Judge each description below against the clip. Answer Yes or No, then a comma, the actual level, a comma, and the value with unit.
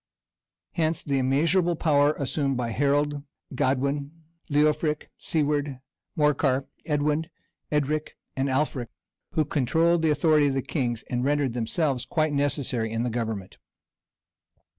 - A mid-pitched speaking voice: Yes, medium, 145 Hz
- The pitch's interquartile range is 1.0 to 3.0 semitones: Yes, narrow, 2.6 semitones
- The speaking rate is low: Yes, slow, 120 wpm